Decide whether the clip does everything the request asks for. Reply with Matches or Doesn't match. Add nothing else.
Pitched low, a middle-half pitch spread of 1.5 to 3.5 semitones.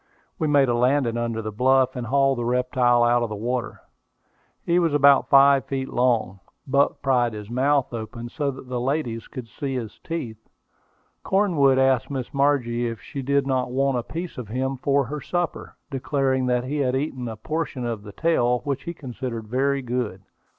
Matches